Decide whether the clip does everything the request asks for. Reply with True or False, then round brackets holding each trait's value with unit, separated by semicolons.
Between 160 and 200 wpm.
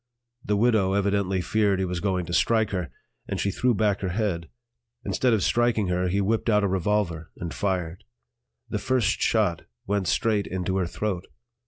True (180 wpm)